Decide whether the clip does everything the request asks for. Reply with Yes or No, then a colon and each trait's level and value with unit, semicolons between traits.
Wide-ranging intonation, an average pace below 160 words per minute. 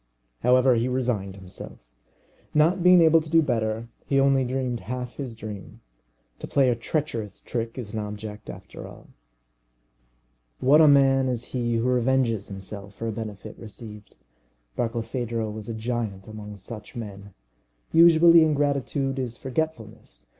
No: average, 3.8 semitones; average, 145 wpm